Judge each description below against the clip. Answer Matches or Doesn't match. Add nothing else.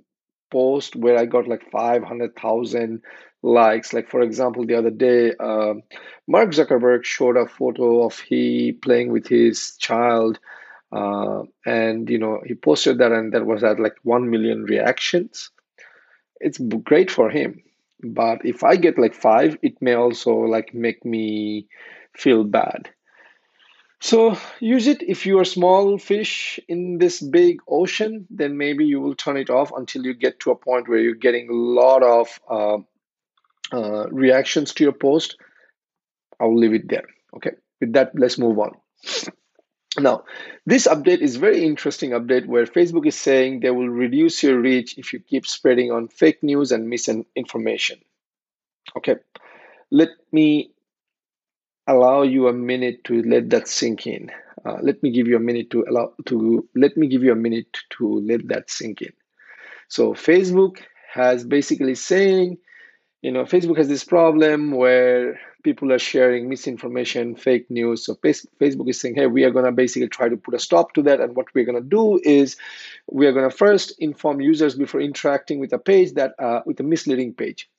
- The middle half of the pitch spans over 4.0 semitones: Matches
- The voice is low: Matches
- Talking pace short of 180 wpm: Matches